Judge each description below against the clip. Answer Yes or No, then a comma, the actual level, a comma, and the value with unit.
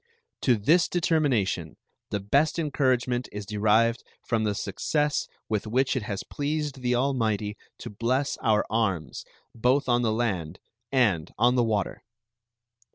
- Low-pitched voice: Yes, low, 120 Hz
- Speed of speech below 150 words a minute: Yes, average, 140 wpm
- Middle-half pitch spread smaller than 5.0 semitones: Yes, average, 4.2 semitones